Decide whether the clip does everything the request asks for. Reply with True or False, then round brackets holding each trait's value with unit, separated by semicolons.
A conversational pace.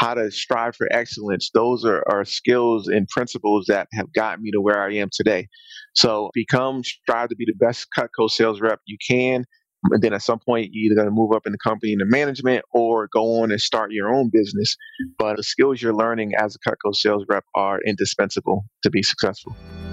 False (215 wpm)